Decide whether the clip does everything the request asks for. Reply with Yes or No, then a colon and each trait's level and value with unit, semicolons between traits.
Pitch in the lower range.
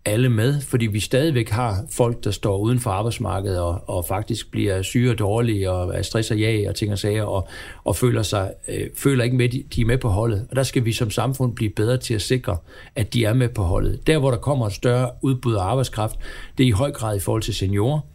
Yes: low, 115 Hz